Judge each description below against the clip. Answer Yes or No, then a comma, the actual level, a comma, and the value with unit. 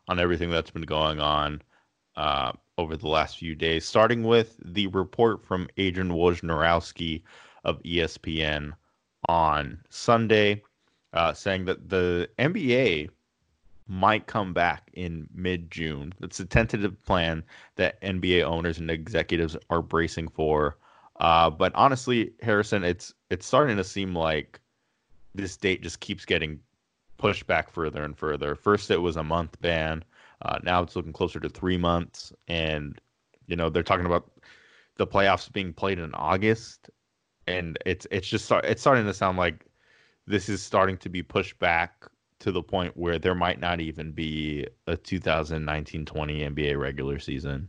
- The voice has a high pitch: No, very low, 85 Hz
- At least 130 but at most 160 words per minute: Yes, average, 155 wpm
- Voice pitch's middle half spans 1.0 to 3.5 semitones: Yes, average, 3.2 semitones